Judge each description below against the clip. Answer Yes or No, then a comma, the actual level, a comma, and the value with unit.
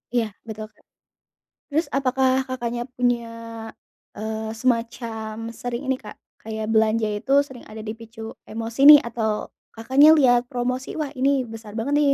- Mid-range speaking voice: No, high, 235 Hz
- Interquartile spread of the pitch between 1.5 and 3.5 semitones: Yes, average, 2.7 semitones